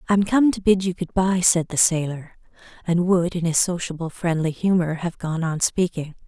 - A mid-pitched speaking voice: Yes, medium, 175 Hz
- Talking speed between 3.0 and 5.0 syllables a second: Yes, 4.9 syllables/s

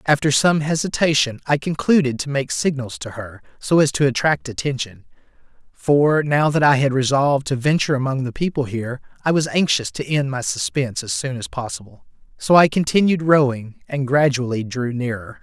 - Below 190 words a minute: Yes, average, 180 wpm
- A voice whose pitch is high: No, low, 135 Hz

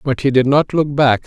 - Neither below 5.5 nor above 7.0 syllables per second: No, 5.3 syllables/s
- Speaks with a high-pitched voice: No, low, 135 Hz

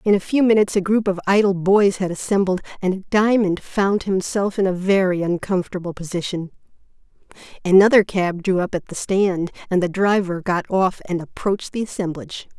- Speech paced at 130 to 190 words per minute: Yes, average, 170 wpm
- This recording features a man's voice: No, female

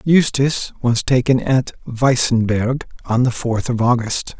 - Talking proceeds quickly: No, slow, 135 wpm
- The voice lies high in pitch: No, low, 125 Hz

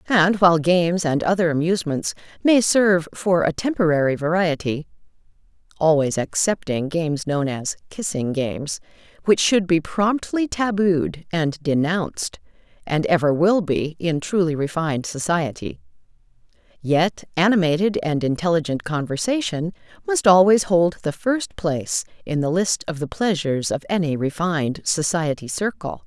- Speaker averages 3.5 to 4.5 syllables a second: Yes, 4.1 syllables/s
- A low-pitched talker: No, medium, 165 Hz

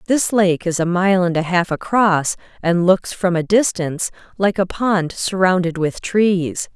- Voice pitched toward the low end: No, medium, 185 Hz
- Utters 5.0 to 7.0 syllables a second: No, 4.2 syllables/s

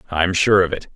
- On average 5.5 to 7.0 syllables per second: Yes, 5.6 syllables/s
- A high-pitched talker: No, very low, 90 Hz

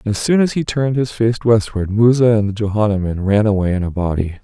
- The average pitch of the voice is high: No, low, 110 Hz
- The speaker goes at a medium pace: No, fast, 245 wpm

